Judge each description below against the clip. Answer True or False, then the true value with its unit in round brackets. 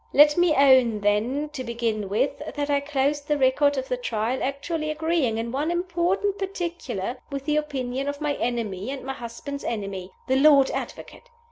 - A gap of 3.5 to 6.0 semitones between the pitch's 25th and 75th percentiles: True (4.1 semitones)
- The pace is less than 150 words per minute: False (175 wpm)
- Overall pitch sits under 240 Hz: False (275 Hz)